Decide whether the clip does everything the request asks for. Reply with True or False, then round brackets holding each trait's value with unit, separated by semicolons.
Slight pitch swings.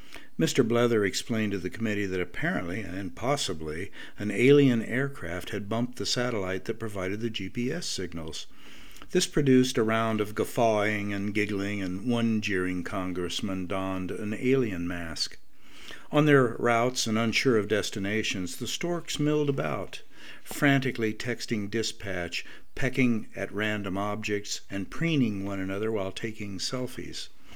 False (4.5 semitones)